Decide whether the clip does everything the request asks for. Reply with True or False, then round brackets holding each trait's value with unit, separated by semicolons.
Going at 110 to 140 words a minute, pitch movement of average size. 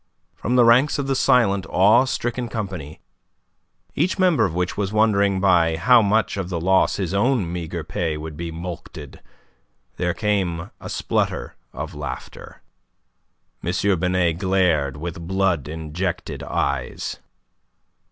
True (135 wpm; 4.1 semitones)